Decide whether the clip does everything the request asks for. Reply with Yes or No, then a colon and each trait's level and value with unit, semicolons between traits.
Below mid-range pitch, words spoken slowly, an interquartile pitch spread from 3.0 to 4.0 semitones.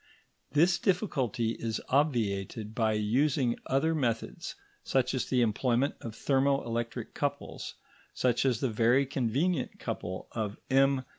Yes: low, 125 Hz; slow, 130 wpm; average, 3.3 semitones